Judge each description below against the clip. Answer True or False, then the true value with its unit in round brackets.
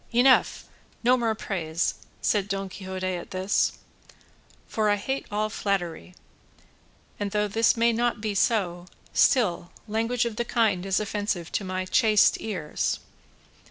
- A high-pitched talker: True (205 Hz)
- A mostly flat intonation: False (3.3 semitones)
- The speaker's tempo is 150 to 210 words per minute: False (140 wpm)